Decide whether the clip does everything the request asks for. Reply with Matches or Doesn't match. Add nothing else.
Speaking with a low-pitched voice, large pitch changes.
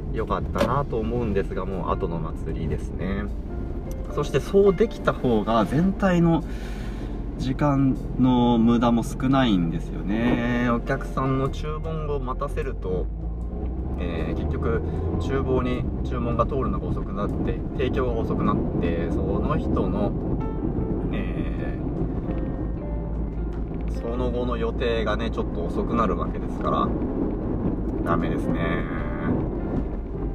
Matches